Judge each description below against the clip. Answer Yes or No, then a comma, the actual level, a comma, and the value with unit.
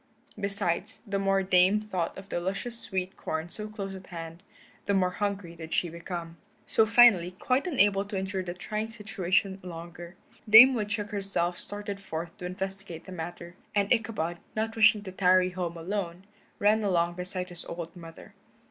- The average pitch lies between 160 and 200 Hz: Yes, high, 190 Hz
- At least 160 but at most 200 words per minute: Yes, average, 175 wpm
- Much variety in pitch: No, average, 2.9 semitones